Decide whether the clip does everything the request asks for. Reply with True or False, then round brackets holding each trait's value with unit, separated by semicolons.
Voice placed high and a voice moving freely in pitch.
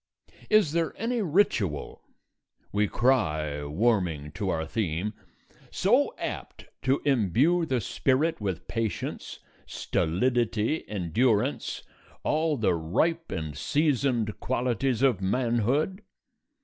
False (120 Hz; 7.2 semitones)